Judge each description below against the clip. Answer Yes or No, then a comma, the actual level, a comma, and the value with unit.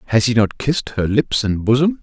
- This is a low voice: Yes, low, 120 Hz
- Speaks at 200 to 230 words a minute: No, fast, 240 wpm